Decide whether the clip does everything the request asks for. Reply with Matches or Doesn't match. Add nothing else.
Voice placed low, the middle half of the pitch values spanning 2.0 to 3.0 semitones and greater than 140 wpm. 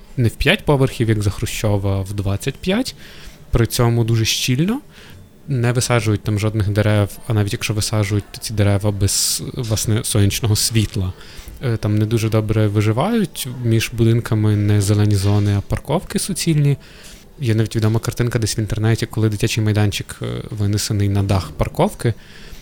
Matches